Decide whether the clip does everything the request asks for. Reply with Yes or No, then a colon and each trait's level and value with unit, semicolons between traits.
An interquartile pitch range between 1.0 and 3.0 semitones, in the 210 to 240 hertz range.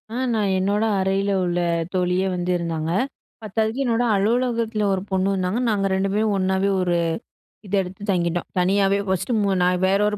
No: narrow, 2.4 semitones; high, 195 Hz